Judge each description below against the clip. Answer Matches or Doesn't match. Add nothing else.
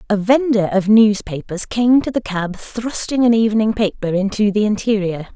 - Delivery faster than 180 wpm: Doesn't match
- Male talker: Doesn't match